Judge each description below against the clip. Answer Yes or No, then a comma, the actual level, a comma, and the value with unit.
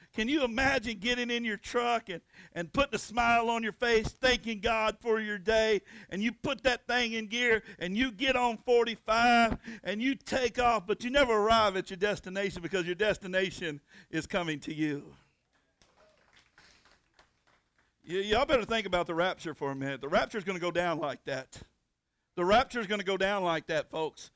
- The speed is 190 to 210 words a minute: Yes, average, 195 wpm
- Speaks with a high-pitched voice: Yes, high, 215 Hz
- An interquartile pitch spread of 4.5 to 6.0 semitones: Yes, average, 5.0 semitones